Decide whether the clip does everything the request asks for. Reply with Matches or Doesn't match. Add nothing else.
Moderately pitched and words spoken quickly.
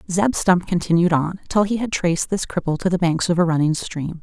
Matches